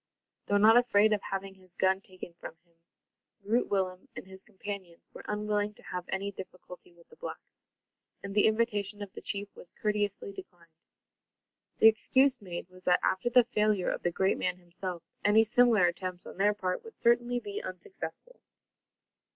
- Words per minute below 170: No, average, 175 wpm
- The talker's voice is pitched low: No, high, 200 Hz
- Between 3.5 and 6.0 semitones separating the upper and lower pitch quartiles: No, average, 3.0 semitones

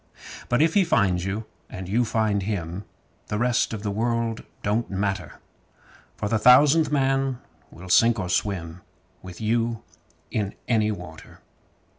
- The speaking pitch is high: No, low, 110 Hz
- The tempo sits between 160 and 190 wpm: No, average, 145 wpm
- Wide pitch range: No, average, 3.6 semitones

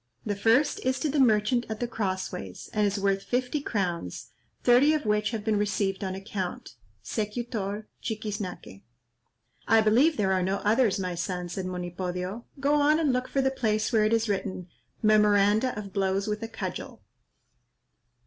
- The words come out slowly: No, average, 170 wpm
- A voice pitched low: No, high, 210 Hz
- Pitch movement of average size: Yes, average, 3.7 semitones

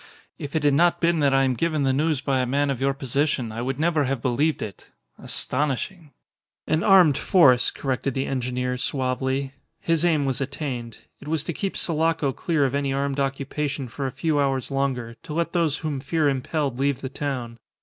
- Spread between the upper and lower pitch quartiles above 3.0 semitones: No, narrow, 2.6 semitones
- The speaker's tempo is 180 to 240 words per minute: Yes, average, 200 wpm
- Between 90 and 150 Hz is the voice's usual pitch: Yes, medium, 140 Hz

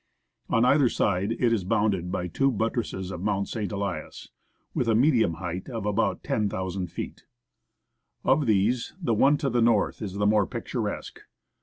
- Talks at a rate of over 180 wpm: No, average, 165 wpm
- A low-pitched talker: Yes, low, 105 Hz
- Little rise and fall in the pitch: No, average, 3.7 semitones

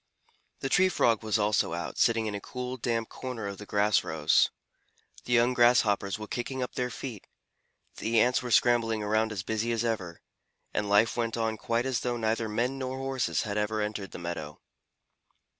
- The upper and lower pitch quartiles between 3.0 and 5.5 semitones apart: No, narrow, 2.6 semitones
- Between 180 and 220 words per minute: Yes, average, 190 wpm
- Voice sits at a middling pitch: No, low, 115 Hz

